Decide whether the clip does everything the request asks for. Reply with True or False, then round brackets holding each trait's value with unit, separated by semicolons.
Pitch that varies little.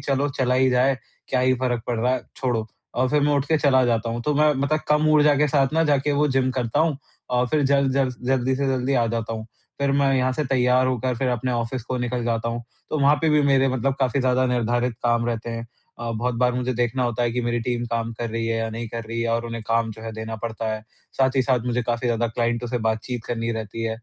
True (2.3 semitones)